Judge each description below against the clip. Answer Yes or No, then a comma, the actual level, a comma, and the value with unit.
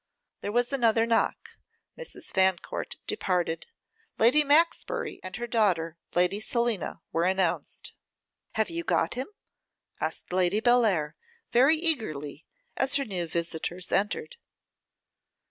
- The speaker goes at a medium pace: No, slow, 115 wpm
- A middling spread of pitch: No, wide, 6.2 semitones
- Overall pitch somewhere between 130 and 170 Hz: No, high, 215 Hz